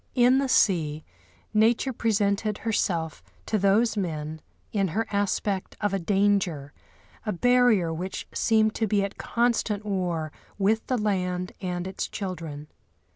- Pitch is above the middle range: Yes, high, 200 Hz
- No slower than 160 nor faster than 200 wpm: No, slow, 135 wpm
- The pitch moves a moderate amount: Yes, average, 3.6 semitones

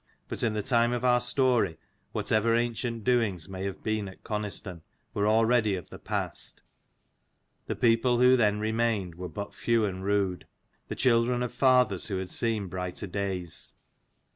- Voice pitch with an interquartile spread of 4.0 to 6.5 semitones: No, average, 3.6 semitones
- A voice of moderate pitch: No, low, 110 Hz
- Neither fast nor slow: Yes, average, 165 wpm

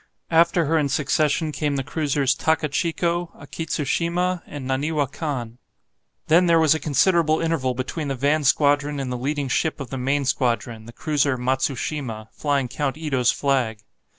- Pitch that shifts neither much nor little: Yes, average, 3.3 semitones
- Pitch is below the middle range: No, medium, 145 Hz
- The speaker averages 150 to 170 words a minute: Yes, average, 155 wpm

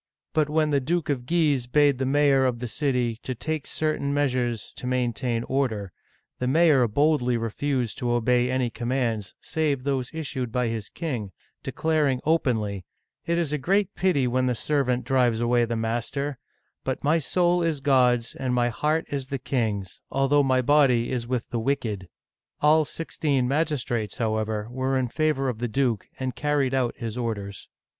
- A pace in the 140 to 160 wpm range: No, average, 175 wpm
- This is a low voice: Yes, low, 130 Hz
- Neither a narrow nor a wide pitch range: Yes, average, 3.4 semitones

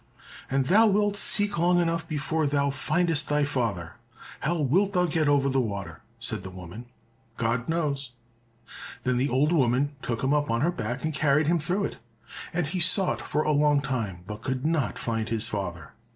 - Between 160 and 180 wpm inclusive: No, average, 190 wpm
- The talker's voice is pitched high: No, medium, 145 Hz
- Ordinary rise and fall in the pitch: No, wide, 5.8 semitones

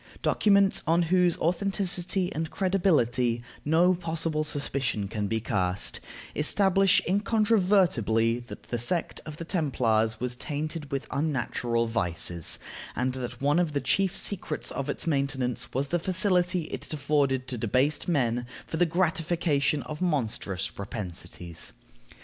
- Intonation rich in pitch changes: Yes, wide, 6.5 semitones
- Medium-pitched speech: Yes, medium, 150 Hz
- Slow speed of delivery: Yes, slow, 130 wpm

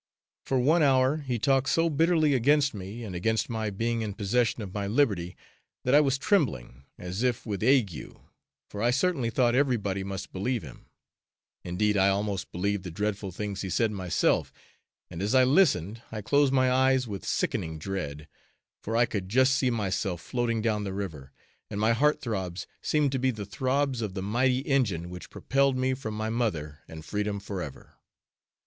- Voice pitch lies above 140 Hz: No, low, 110 Hz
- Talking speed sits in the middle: Yes, average, 180 wpm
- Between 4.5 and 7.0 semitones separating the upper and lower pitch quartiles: Yes, average, 5.0 semitones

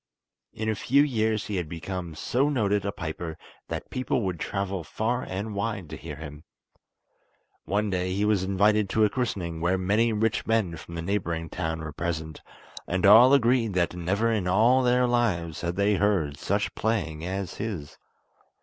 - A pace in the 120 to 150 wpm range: No, average, 175 wpm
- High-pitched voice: No, low, 100 Hz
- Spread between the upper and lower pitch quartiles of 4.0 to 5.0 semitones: Yes, average, 4.5 semitones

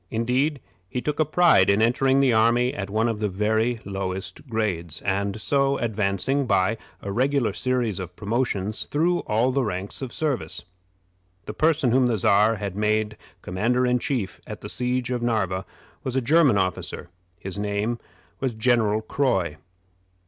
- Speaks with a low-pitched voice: Yes, low, 115 Hz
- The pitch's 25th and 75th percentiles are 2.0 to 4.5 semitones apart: Yes, average, 4.1 semitones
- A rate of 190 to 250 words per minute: No, average, 165 wpm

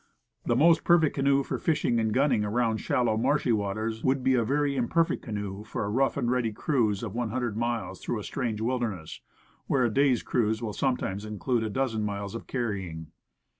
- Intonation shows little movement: No, average, 3.6 semitones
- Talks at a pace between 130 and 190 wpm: No, fast, 205 wpm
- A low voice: Yes, low, 115 Hz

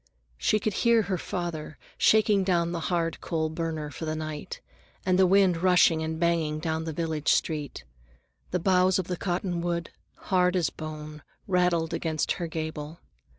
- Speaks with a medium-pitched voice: Yes, medium, 170 Hz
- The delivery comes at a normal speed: Yes, average, 160 wpm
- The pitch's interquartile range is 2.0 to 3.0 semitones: Yes, narrow, 2.4 semitones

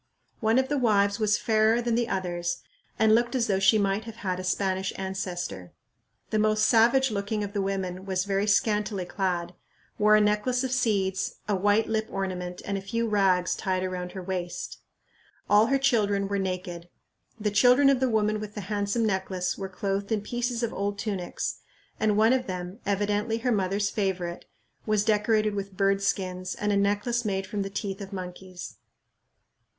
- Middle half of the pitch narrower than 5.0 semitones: Yes, narrow, 2.4 semitones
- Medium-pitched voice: No, high, 200 Hz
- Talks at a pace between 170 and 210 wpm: Yes, average, 185 wpm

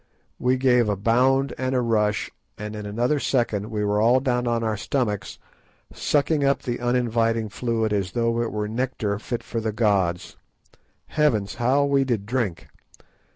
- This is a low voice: Yes, low, 115 Hz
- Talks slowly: No, average, 165 wpm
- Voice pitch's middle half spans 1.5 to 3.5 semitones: Yes, average, 3.2 semitones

